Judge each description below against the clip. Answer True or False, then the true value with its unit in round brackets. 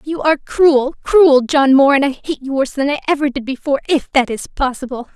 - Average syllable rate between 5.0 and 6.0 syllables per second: True (5.9 syllables/s)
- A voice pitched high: True (280 Hz)